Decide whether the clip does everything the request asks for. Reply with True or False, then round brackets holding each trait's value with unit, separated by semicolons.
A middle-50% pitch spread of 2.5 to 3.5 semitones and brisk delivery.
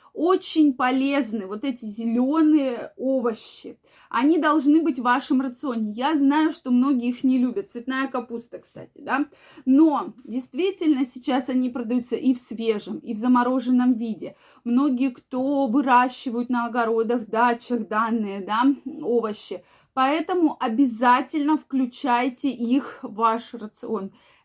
False (2.8 semitones; 125 wpm)